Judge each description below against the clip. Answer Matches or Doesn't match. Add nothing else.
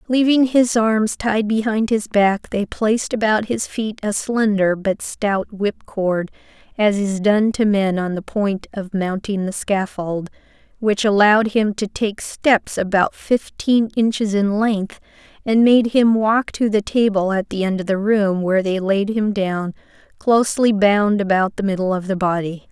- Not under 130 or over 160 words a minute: Doesn't match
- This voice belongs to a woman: Matches